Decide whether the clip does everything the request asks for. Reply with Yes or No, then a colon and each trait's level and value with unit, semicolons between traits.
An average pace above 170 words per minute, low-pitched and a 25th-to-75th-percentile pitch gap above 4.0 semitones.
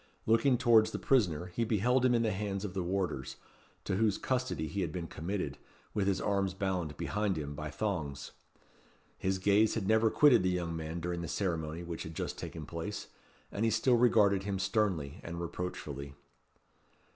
Yes: average, 180 wpm; very low, 95 Hz; average, 4.5 semitones